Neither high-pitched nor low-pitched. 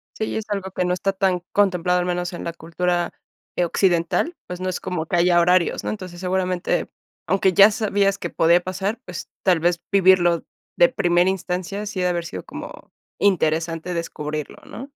Yes: medium, 180 Hz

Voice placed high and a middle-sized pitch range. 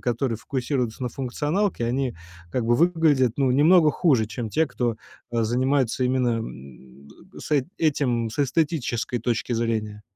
No: low, 125 Hz; average, 3.6 semitones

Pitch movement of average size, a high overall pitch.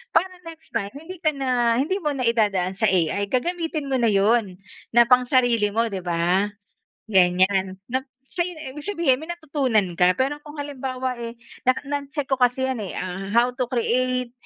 No: wide, 5.8 semitones; very high, 250 Hz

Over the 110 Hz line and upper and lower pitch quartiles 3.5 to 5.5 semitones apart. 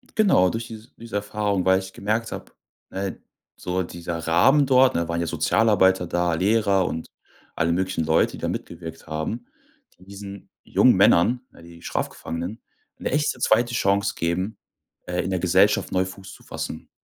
No: very low, 95 Hz; average, 4.2 semitones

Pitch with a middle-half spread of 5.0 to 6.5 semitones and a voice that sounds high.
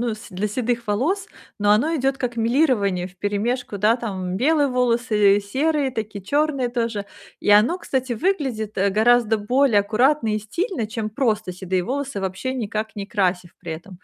No: average, 4.3 semitones; high, 225 Hz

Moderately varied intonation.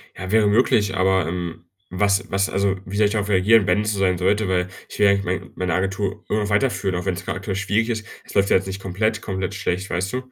No: narrow, 2.0 semitones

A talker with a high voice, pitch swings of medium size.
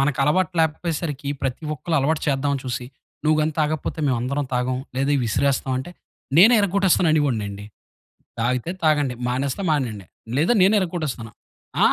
No: medium, 145 Hz; average, 3.9 semitones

